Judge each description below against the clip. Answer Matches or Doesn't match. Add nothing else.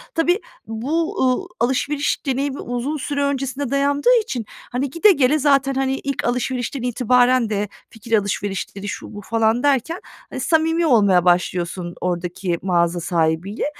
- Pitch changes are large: Matches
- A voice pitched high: Matches